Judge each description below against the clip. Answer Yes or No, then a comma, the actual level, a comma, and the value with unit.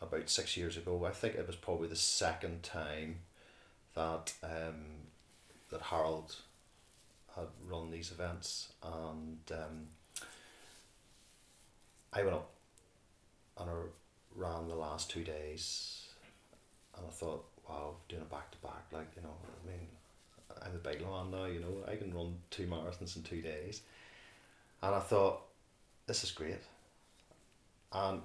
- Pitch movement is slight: Yes, narrow, 2.1 semitones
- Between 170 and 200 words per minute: No, average, 145 wpm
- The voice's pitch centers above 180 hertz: No, very low, 85 Hz